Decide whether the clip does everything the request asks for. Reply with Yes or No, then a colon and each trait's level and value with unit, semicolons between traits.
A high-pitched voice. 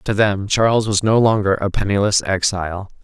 No: low, 100 Hz